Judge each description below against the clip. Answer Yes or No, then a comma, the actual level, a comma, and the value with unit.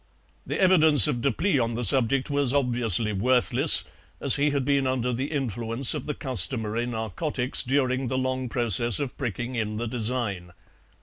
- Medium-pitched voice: No, low, 125 Hz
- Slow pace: No, average, 165 wpm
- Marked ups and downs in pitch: No, average, 2.9 semitones